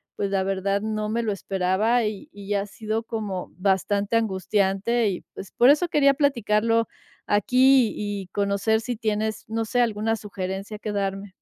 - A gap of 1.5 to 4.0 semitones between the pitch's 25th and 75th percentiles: Yes, narrow, 2.4 semitones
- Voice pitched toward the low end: No, high, 210 Hz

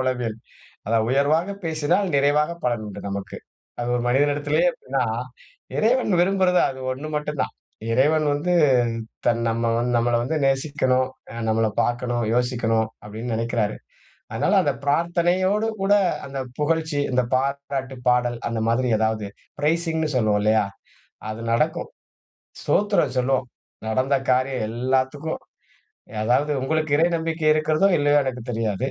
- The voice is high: No, low, 135 Hz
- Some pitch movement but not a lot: Yes, average, 4.6 semitones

